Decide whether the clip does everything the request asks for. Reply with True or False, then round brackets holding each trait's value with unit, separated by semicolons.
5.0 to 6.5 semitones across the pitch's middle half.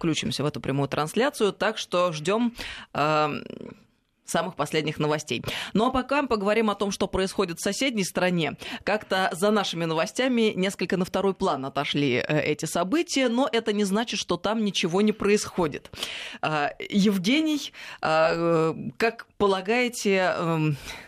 True (5.3 semitones)